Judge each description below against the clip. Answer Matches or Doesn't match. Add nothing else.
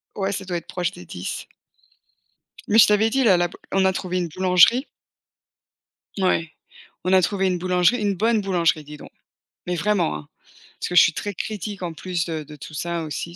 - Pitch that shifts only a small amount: Doesn't match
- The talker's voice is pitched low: Doesn't match